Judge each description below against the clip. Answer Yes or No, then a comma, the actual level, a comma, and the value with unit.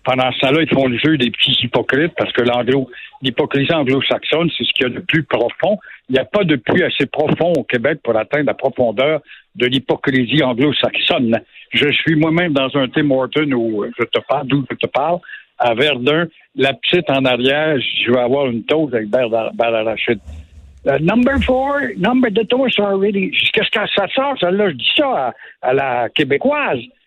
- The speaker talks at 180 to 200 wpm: Yes, average, 195 wpm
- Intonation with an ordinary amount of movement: No, wide, 5.7 semitones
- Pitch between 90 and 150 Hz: Yes, medium, 140 Hz